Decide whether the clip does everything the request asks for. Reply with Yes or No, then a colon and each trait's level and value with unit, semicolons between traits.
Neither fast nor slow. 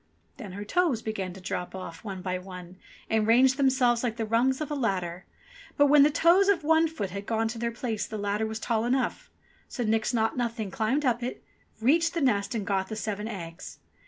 No: fast, 220 wpm